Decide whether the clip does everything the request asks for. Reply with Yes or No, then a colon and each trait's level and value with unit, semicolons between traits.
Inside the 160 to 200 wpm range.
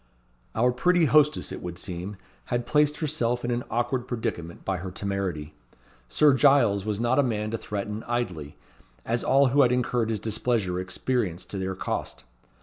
Yes: average, 170 wpm